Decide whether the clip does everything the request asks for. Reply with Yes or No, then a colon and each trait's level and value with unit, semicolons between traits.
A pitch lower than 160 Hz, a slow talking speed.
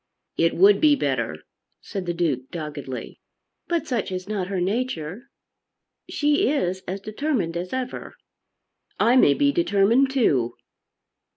No: high, 195 Hz; slow, 130 wpm